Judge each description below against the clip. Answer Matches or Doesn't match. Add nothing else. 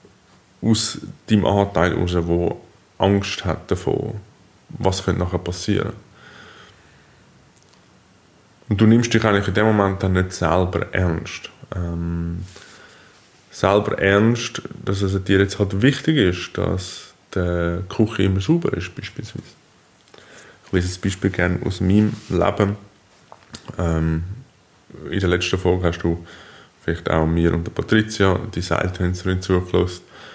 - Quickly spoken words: Doesn't match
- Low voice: Matches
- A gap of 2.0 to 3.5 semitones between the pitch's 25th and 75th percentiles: Matches